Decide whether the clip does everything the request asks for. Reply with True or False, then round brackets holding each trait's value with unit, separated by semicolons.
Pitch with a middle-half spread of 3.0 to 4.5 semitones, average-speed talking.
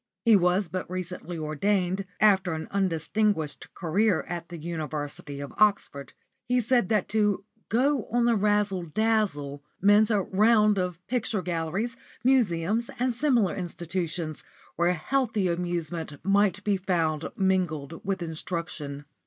False (4.2 semitones; 130 wpm)